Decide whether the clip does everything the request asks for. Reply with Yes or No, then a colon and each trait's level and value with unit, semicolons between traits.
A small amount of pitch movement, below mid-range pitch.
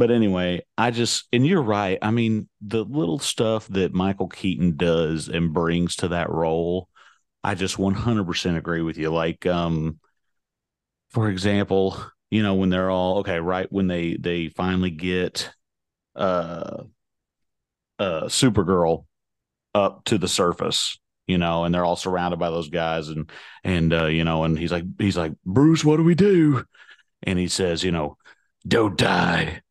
No: average, 3.5 semitones; very low, 90 Hz